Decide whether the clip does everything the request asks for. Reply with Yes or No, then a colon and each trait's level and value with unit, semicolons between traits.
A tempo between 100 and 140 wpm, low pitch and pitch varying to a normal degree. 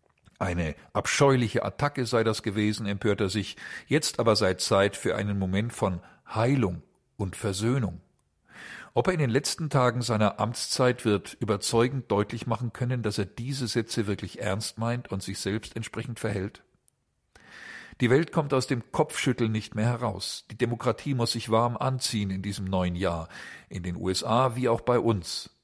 No: average, 165 wpm; low, 115 Hz; average, 3.6 semitones